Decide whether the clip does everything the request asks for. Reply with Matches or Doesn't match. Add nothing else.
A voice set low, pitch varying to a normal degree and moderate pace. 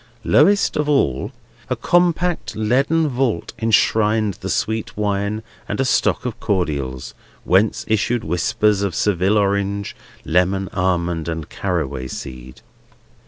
Doesn't match